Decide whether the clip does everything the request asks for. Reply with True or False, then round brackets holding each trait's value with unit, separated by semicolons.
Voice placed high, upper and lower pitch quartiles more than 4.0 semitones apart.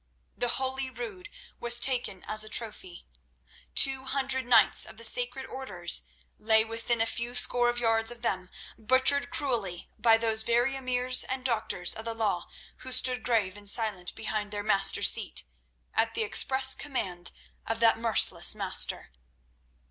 False (235 Hz; 3.1 semitones)